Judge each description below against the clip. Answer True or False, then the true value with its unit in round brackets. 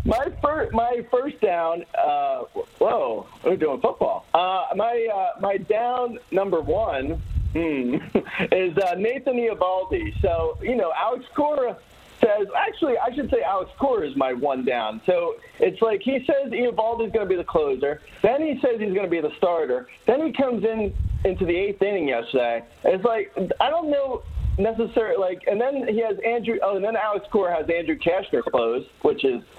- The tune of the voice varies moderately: False (7.8 semitones)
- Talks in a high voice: True (230 Hz)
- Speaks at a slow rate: False (185 wpm)